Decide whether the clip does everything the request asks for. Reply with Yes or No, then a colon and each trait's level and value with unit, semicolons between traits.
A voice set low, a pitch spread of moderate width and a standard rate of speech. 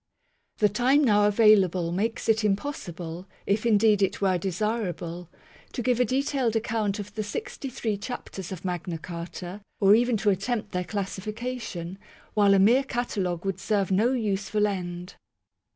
No: high, 205 Hz; average, 3.4 semitones; average, 155 wpm